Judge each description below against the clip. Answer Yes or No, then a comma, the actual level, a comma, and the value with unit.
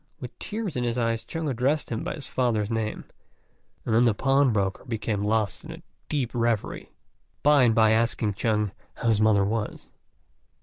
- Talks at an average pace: Yes, average, 175 wpm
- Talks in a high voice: No, low, 115 Hz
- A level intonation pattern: No, average, 3.3 semitones